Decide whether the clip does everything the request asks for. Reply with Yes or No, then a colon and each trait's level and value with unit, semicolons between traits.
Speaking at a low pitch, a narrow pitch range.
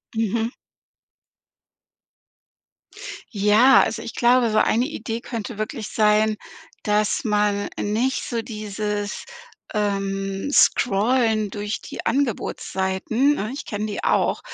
No: high, 215 Hz; narrow, 2.2 semitones